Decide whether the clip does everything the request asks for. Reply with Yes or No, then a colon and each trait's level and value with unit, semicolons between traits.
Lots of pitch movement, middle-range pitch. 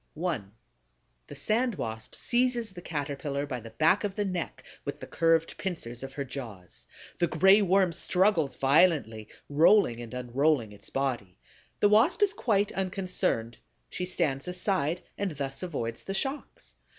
Yes: wide, 6.4 semitones; medium, 165 Hz